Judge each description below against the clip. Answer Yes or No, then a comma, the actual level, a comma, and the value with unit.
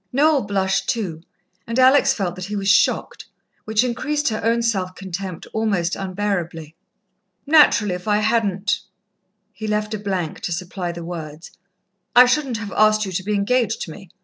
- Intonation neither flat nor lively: Yes, average, 3.8 semitones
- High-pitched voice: Yes, high, 205 Hz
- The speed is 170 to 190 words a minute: Yes, average, 175 wpm